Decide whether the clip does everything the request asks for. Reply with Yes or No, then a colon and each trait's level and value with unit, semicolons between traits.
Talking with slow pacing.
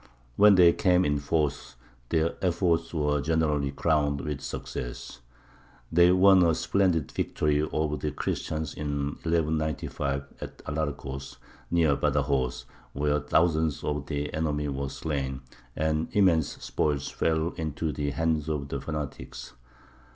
Yes: slow, 130 wpm